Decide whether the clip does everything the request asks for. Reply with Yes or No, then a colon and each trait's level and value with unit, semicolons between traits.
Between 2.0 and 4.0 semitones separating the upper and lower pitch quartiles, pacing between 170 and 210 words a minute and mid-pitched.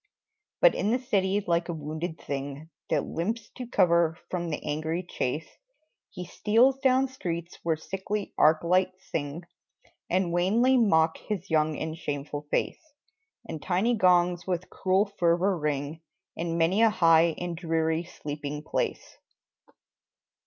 No: average, 3.5 semitones; average, 140 wpm; medium, 170 Hz